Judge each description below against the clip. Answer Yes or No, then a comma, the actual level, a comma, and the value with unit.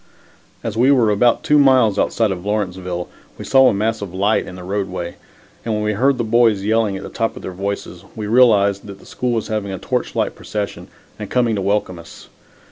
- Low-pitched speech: Yes, low, 105 Hz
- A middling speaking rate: No, fast, 220 wpm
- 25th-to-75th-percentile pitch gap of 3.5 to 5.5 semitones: No, average, 2.8 semitones